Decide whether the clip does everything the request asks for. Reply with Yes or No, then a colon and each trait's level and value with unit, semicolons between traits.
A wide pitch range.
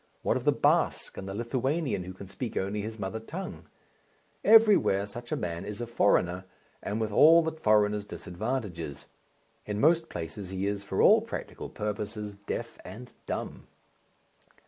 No: average, 3.9 semitones